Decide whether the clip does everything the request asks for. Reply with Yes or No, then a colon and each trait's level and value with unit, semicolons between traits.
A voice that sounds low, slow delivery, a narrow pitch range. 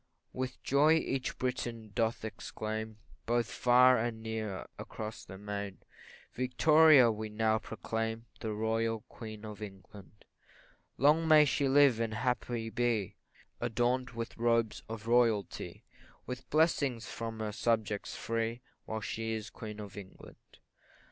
Yes: low, 115 Hz; slow, 130 wpm; narrow, 2.3 semitones